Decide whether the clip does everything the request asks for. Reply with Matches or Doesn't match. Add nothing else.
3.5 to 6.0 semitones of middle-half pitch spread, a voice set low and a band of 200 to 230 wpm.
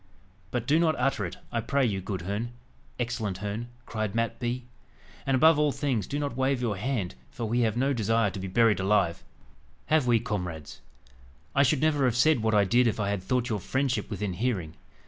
Matches